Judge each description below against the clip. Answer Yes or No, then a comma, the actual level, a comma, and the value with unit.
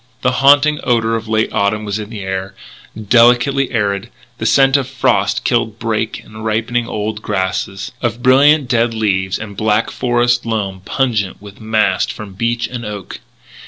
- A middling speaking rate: Yes, average, 160 wpm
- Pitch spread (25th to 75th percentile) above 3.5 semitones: No, average, 2.9 semitones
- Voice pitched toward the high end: No, low, 110 Hz